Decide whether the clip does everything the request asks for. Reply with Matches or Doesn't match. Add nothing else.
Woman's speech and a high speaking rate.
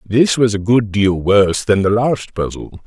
Doesn't match